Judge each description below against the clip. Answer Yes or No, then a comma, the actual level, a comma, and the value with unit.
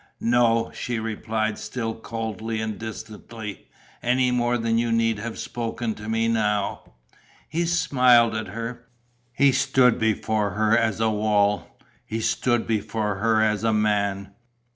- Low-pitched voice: Yes, low, 115 Hz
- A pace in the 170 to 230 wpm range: No, average, 140 wpm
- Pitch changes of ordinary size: No, narrow, 1.5 semitones